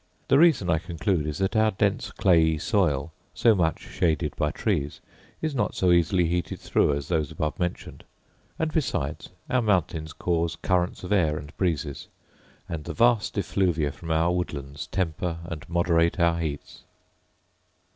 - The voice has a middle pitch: No, very low, 85 Hz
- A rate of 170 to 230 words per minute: No, average, 155 wpm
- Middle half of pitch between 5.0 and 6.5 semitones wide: No, average, 3.3 semitones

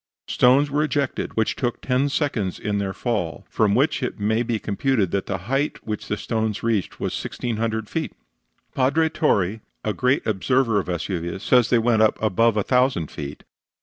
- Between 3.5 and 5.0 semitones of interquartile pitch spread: Yes, average, 4.1 semitones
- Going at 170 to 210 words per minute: Yes, average, 180 wpm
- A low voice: Yes, low, 110 Hz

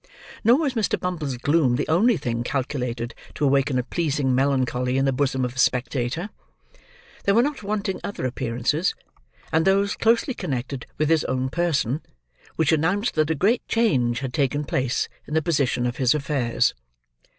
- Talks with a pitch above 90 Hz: Yes, medium, 140 Hz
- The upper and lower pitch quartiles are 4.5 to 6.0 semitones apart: Yes, wide, 5.4 semitones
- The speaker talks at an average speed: Yes, average, 170 wpm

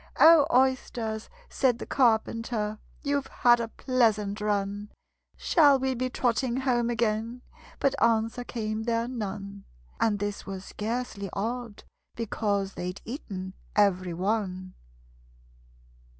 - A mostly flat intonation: No, average, 3.4 semitones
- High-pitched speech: Yes, high, 225 Hz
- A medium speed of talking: No, slow, 115 wpm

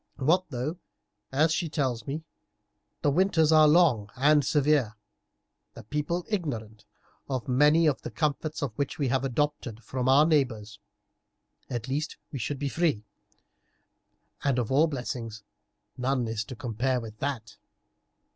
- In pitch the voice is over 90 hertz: Yes, low, 135 Hz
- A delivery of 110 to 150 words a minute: Yes, average, 140 wpm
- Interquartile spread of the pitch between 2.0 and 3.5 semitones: No, average, 4.0 semitones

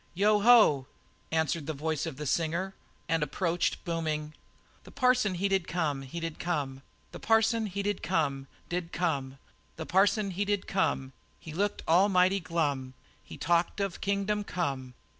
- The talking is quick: No, average, 160 wpm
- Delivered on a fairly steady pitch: No, average, 4.6 semitones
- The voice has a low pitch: No, medium, 170 Hz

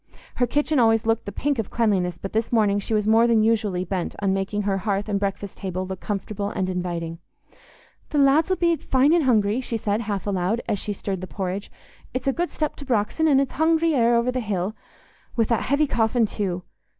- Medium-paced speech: No, fast, 215 wpm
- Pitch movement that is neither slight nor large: Yes, average, 4.3 semitones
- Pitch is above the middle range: Yes, high, 215 Hz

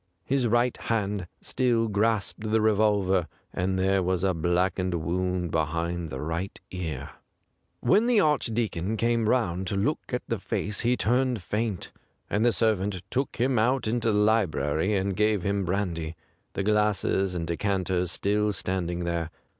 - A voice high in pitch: No, low, 100 Hz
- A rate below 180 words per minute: Yes, average, 155 wpm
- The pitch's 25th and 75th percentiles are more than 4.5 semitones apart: No, average, 3.9 semitones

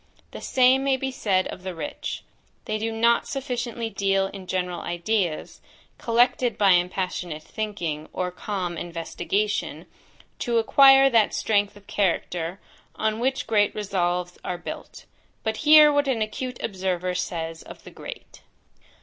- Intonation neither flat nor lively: Yes, average, 4.6 semitones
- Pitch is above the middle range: Yes, high, 205 Hz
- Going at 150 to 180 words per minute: No, average, 140 wpm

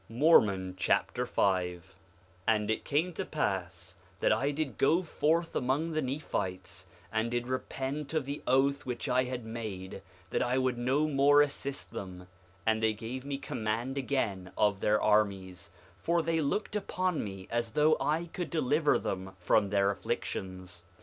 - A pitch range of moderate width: No, wide, 6.6 semitones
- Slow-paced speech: No, average, 165 wpm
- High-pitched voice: No, low, 120 Hz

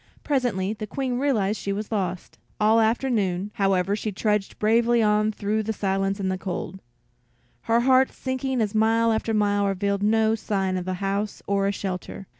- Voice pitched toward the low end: No, high, 210 Hz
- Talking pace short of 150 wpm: No, average, 180 wpm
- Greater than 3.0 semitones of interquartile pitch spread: No, narrow, 2.4 semitones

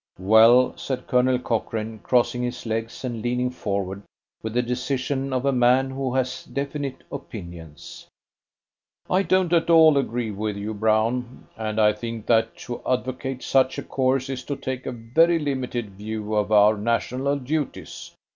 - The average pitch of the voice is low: Yes, low, 125 Hz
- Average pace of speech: Yes, average, 155 wpm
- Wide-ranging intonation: No, average, 3.2 semitones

